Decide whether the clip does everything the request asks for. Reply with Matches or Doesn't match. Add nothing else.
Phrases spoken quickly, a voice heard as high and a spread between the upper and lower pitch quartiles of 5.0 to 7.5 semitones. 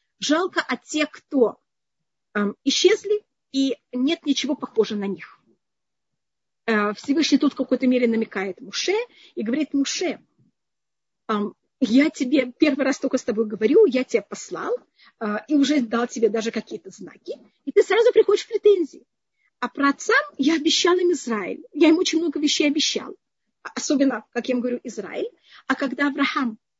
Matches